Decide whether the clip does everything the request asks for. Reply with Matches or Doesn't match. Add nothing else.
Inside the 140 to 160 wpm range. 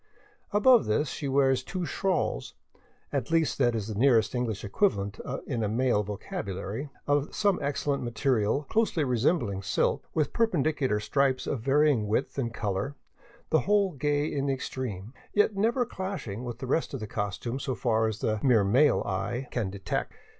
Doesn't match